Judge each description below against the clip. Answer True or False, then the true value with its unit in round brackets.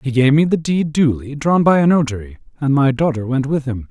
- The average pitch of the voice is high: False (140 Hz)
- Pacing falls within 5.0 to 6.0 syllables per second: True (5.5 syllables/s)